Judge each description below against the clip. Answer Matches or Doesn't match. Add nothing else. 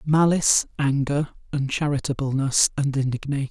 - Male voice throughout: Matches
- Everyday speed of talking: Doesn't match